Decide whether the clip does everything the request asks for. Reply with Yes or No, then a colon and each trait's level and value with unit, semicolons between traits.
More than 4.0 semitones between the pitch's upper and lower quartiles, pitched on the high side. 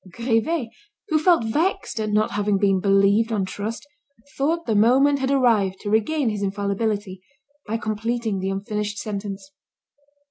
No: average, 3.3 semitones; high, 215 Hz